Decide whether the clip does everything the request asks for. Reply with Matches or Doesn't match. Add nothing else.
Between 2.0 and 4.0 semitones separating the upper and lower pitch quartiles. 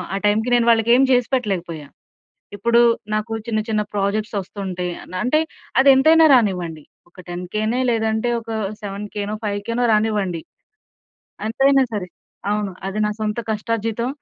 Matches